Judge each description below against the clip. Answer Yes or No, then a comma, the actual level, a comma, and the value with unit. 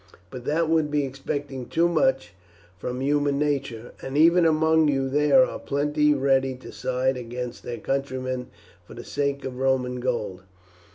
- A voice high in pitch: No, low, 135 Hz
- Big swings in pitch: No, narrow, 2.6 semitones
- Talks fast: No, average, 160 wpm